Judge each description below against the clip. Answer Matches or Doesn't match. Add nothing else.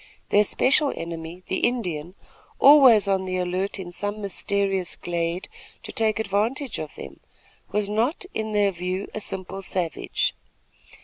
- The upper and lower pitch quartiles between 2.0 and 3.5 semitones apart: Matches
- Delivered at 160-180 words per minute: Doesn't match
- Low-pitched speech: Doesn't match